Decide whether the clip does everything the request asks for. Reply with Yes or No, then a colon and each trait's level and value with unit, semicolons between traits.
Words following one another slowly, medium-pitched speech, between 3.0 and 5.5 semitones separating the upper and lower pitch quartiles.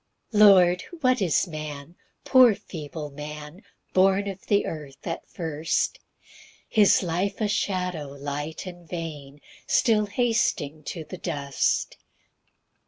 Yes: slow, 120 wpm; medium, 170 Hz; average, 5.1 semitones